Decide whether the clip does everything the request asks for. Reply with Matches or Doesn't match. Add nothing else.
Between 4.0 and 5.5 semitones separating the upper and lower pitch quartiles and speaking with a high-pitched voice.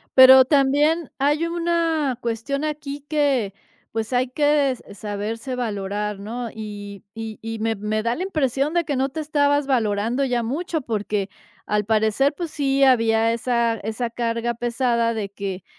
Matches